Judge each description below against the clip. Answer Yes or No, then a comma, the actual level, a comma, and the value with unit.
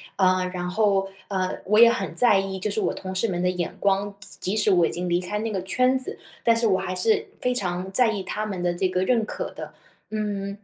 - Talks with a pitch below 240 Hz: Yes, high, 195 Hz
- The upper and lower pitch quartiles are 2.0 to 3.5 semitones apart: Yes, average, 2.8 semitones